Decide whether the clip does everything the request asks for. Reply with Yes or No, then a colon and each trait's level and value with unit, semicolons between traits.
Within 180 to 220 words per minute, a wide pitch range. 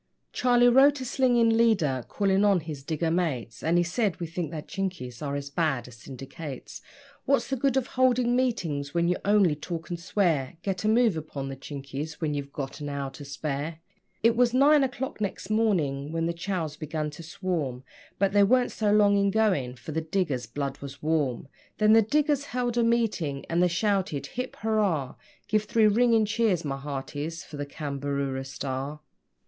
Yes: average, 190 wpm; wide, 7.4 semitones